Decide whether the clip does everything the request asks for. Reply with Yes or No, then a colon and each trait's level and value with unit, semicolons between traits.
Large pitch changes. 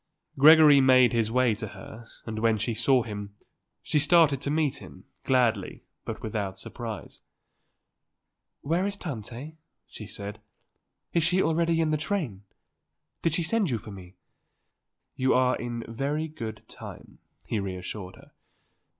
Yes: wide, 6.1 semitones